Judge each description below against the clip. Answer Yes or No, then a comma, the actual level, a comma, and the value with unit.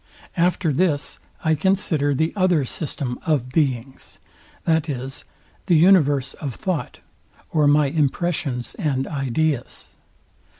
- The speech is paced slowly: Yes, slow, 110 wpm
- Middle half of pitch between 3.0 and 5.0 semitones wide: Yes, average, 3.5 semitones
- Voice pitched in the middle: Yes, medium, 150 Hz